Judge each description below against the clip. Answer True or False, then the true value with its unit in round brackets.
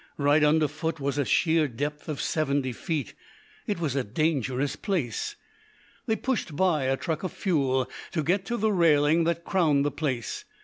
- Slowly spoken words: False (175 wpm)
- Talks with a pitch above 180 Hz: False (150 Hz)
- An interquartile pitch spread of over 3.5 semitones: False (3.2 semitones)